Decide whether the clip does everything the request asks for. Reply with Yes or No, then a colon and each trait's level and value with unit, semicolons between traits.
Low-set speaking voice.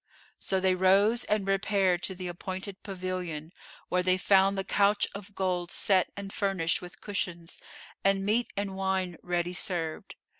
No: high, 190 Hz